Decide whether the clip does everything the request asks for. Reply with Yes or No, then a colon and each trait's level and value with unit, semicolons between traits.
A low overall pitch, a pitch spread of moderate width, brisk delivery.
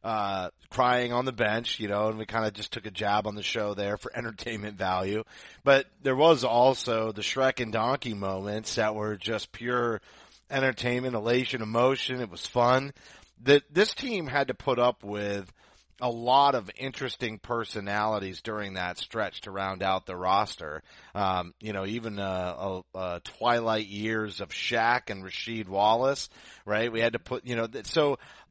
No: low, 110 Hz; average, 3.5 semitones; average, 175 wpm